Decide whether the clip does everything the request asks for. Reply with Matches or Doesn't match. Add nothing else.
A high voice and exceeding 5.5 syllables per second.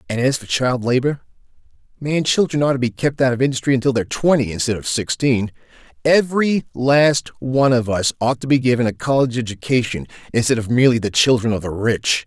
Doesn't match